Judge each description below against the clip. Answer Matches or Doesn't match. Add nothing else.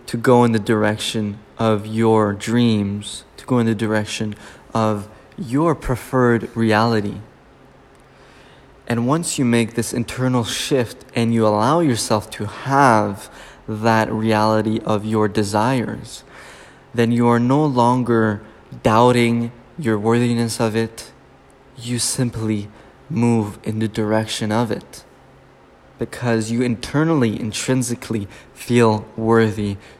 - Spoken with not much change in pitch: Matches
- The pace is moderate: Doesn't match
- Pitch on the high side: Doesn't match